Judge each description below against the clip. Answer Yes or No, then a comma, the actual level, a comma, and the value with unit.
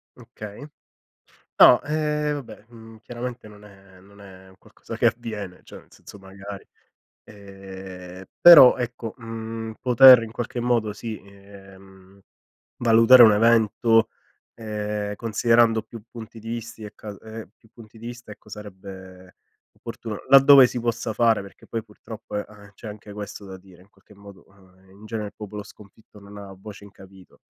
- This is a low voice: Yes, low, 105 Hz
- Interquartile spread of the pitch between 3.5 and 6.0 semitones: No, average, 2.7 semitones